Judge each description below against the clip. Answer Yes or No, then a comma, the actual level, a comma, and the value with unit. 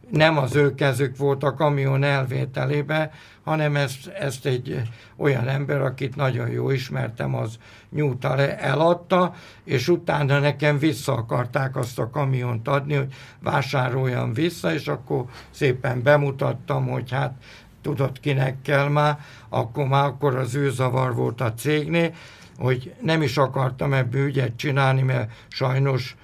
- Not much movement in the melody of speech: Yes, narrow, 2.1 semitones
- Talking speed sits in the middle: Yes, average, 140 wpm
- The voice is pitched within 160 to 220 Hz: No, low, 135 Hz